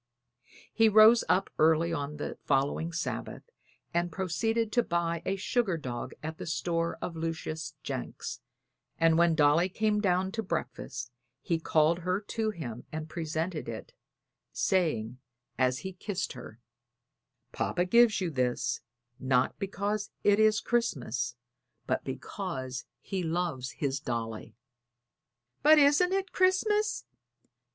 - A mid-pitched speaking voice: Yes, medium, 170 Hz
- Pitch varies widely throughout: Yes, wide, 6.0 semitones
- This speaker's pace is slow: Yes, slow, 130 wpm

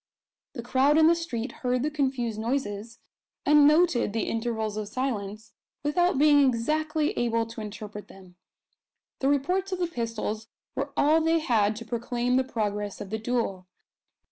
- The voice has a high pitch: Yes, high, 240 Hz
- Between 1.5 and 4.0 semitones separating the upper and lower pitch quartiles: No, average, 5.1 semitones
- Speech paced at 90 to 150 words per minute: No, average, 160 wpm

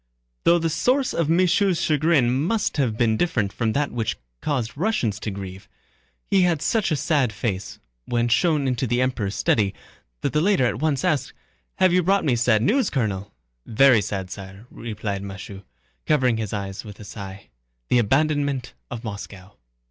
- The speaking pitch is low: Yes, low, 125 Hz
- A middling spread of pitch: No, wide, 6.9 semitones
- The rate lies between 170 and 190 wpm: Yes, average, 175 wpm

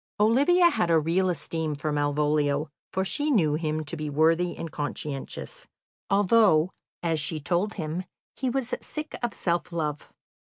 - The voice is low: No, medium, 165 Hz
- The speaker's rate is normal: Yes, average, 155 wpm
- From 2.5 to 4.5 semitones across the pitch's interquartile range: No, average, 5.2 semitones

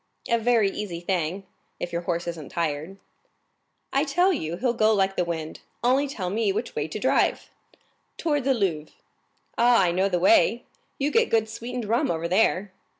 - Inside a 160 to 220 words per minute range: Yes, average, 170 wpm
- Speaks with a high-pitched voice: Yes, high, 200 Hz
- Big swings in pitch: Yes, wide, 6.0 semitones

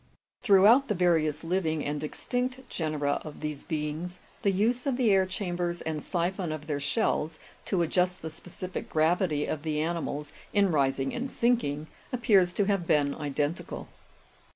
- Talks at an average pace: Yes, average, 160 wpm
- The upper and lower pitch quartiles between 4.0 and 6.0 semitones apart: Yes, average, 4.5 semitones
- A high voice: No, medium, 170 Hz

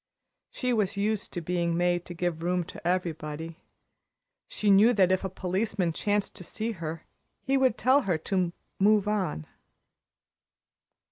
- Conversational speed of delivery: Yes, average, 150 wpm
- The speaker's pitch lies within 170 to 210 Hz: Yes, medium, 185 Hz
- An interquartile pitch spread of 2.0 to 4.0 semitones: Yes, average, 3.4 semitones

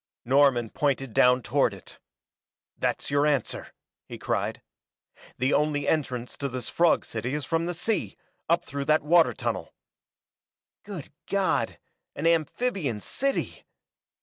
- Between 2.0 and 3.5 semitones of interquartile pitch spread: No, average, 4.5 semitones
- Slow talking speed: Yes, slow, 130 wpm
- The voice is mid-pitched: Yes, medium, 145 Hz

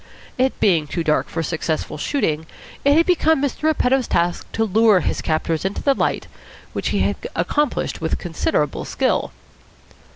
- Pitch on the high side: Yes, high, 195 Hz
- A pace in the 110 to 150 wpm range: No, average, 160 wpm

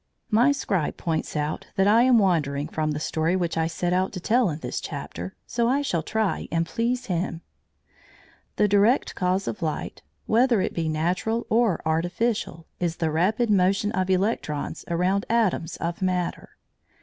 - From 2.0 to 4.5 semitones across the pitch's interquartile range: No, average, 5.0 semitones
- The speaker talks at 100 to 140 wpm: No, average, 170 wpm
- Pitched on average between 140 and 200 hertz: Yes, medium, 185 Hz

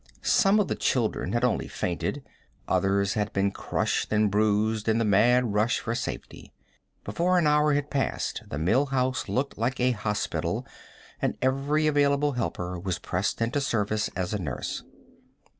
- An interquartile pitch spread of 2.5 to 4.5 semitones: No, average, 5.0 semitones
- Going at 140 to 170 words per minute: Yes, average, 160 wpm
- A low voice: Yes, low, 115 Hz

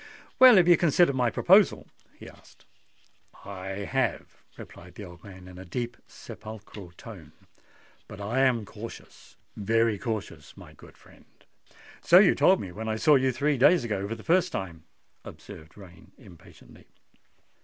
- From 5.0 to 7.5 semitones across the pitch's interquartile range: Yes, wide, 5.6 semitones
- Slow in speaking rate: No, average, 155 wpm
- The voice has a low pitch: Yes, low, 110 Hz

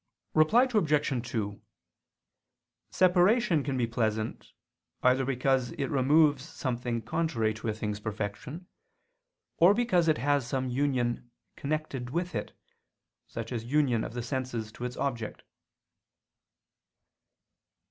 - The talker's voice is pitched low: Yes, low, 130 Hz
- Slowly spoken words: Yes, slow, 115 wpm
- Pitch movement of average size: Yes, average, 4.8 semitones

